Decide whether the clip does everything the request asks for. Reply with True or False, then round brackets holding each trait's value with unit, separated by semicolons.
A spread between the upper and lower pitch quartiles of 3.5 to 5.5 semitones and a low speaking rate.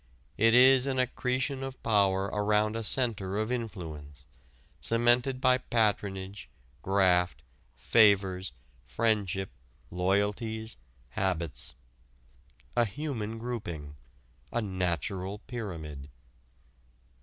True (4.2 semitones; 85 wpm)